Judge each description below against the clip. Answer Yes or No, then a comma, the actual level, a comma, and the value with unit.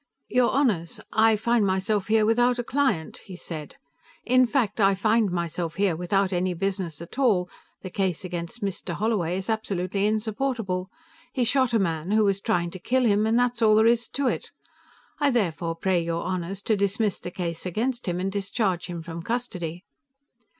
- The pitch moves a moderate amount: Yes, average, 4.3 semitones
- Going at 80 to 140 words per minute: No, average, 185 wpm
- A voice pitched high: Yes, high, 200 Hz